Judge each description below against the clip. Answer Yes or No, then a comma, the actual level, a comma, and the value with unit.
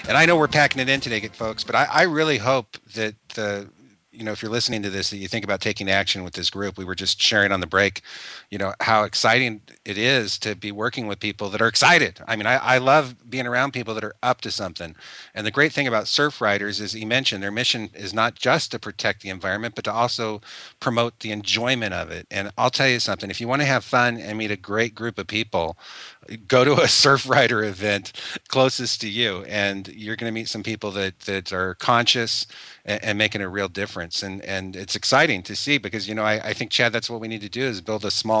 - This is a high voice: No, low, 110 Hz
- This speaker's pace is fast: Yes, fast, 250 wpm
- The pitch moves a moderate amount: Yes, average, 3.1 semitones